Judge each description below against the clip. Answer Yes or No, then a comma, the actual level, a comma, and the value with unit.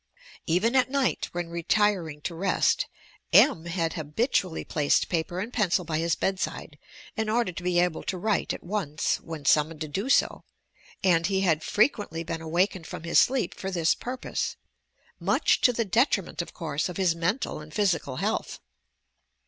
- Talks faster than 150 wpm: Yes, average, 175 wpm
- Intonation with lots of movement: No, average, 4.1 semitones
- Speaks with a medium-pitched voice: Yes, medium, 175 Hz